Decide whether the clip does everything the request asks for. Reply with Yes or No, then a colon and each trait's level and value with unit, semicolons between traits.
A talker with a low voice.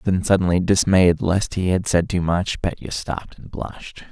Yes: very low, 90 Hz